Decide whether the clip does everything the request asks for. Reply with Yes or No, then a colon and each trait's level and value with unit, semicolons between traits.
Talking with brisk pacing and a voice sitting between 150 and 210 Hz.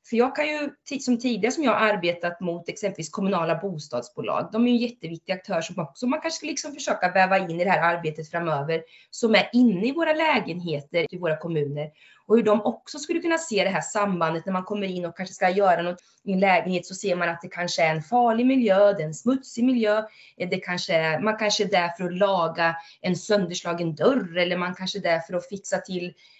Yes: fast, 230 wpm; high, 190 Hz